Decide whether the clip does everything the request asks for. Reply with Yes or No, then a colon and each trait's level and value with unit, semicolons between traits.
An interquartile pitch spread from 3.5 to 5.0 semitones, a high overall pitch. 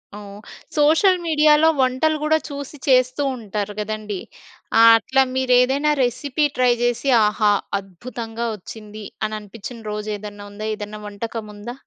Yes: average, 4.3 semitones; high, 230 Hz